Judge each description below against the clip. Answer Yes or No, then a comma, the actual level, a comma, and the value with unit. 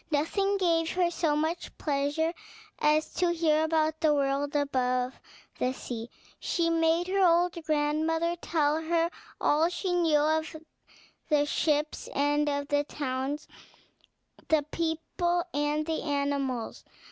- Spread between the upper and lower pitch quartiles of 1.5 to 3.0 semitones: Yes, narrow, 2.5 semitones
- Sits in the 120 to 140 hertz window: No, very high, 310 Hz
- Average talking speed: No, slow, 130 wpm